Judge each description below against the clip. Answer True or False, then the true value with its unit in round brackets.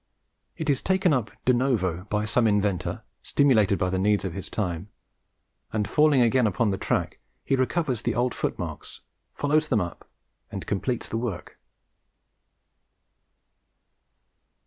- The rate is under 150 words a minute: True (140 wpm)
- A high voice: False (110 Hz)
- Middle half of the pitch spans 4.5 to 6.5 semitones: True (4.9 semitones)